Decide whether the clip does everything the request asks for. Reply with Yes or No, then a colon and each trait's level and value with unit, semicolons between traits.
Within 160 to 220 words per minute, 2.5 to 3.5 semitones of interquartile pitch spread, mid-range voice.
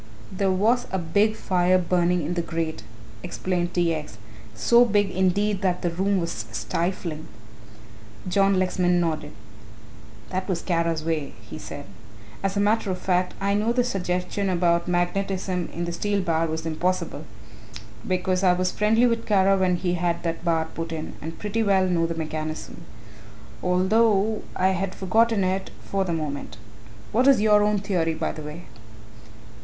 Yes: average, 165 wpm; average, 2.8 semitones; medium, 180 Hz